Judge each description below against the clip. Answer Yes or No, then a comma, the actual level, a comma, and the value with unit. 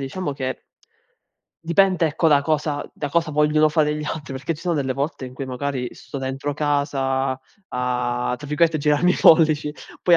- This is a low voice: No, medium, 145 Hz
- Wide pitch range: No, average, 2.7 semitones